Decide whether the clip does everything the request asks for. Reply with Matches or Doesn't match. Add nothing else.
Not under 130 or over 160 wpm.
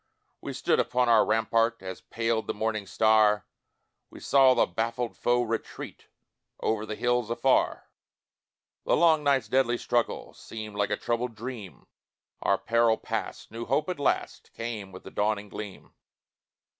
Matches